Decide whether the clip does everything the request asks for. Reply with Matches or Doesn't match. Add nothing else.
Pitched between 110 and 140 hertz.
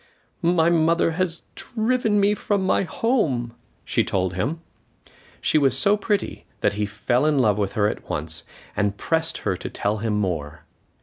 Matches